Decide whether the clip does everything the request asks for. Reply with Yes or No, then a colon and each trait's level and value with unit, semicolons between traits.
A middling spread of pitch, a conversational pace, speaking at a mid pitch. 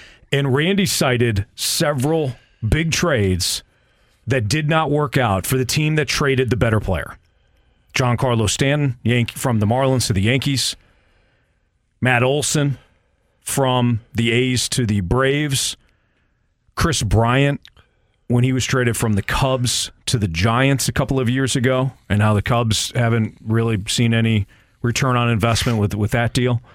No: average, 3.5 semitones; average, 155 wpm; low, 120 Hz